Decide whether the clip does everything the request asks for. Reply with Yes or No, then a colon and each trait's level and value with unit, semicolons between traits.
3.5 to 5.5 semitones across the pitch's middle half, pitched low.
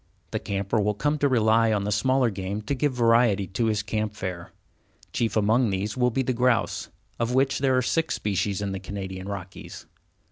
Yes: average, 3.8 semitones; low, 110 Hz